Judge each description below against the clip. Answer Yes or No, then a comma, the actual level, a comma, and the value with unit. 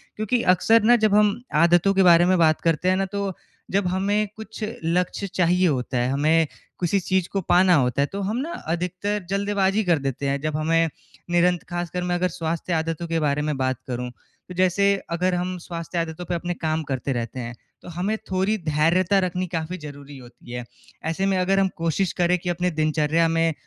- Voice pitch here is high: No, medium, 175 Hz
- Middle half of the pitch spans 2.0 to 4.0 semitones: Yes, average, 3.2 semitones